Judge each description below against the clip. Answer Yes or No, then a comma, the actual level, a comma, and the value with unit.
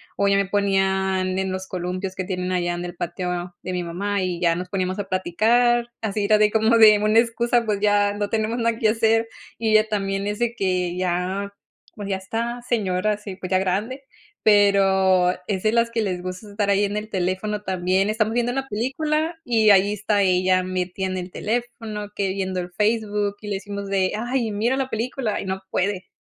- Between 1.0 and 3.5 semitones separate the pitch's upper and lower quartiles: Yes, average, 2.9 semitones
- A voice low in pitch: No, high, 200 Hz